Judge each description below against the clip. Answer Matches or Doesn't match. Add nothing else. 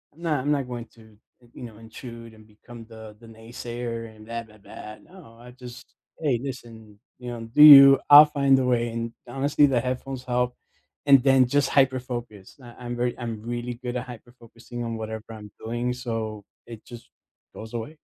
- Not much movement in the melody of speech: Matches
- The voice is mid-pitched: Doesn't match